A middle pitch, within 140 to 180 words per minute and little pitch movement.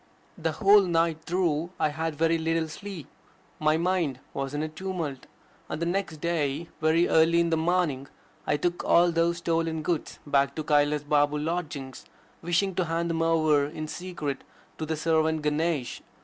Yes: medium, 160 Hz; average, 170 wpm; narrow, 2.1 semitones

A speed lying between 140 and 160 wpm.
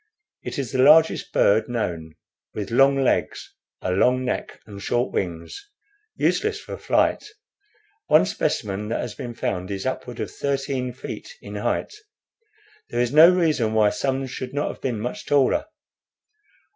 Yes: average, 155 wpm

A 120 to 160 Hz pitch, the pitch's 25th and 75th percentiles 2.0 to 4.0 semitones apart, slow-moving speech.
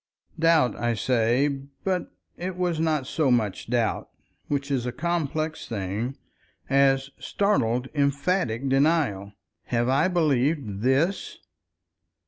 No: medium, 140 Hz; average, 5.0 semitones; slow, 105 wpm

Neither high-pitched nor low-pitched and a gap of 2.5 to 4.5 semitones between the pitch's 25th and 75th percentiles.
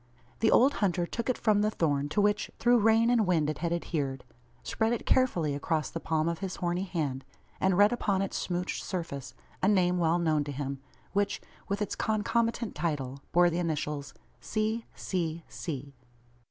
No: medium, 175 Hz; average, 5.2 semitones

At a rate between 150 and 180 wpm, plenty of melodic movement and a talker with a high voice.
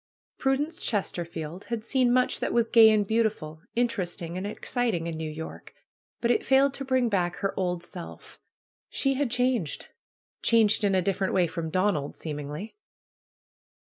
Yes: average, 155 wpm; wide, 6.1 semitones; high, 205 Hz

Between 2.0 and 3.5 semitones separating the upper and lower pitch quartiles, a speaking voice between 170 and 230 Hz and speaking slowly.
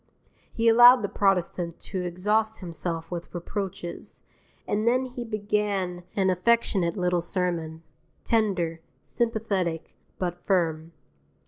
No: average, 3.9 semitones; medium, 185 Hz; slow, 110 wpm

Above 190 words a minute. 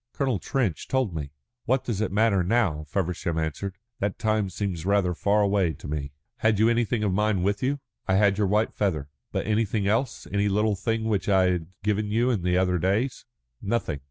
Yes: average, 200 wpm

